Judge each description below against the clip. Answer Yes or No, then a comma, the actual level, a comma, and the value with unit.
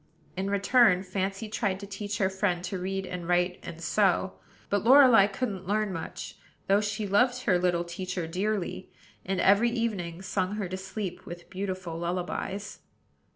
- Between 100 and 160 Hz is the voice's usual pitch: No, high, 190 Hz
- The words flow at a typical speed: Yes, average, 160 wpm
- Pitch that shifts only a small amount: Yes, narrow, 2.3 semitones